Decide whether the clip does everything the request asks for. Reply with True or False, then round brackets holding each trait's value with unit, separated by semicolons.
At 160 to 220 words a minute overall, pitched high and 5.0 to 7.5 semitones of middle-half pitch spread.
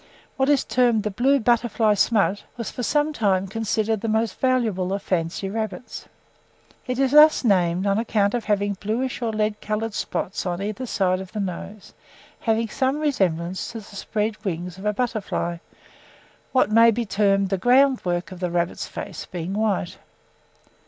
False (170 wpm; 215 Hz; 3.7 semitones)